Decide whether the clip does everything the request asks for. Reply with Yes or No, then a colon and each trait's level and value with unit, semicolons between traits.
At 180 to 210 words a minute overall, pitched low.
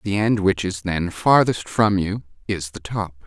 Yes: average, 200 wpm; low, 100 Hz